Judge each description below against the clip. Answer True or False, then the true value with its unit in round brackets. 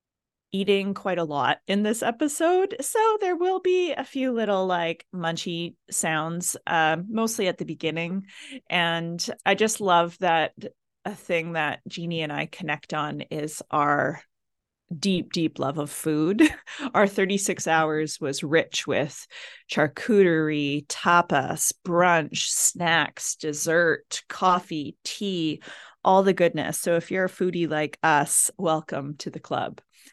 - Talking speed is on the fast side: False (135 wpm)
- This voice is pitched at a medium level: True (175 Hz)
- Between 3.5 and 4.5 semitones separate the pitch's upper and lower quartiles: True (4.2 semitones)